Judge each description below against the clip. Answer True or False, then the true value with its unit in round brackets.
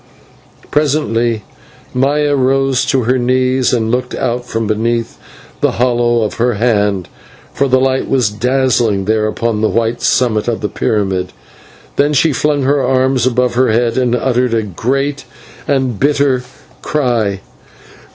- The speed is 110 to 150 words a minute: True (145 wpm)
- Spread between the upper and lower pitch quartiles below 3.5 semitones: True (2.8 semitones)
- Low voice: True (125 Hz)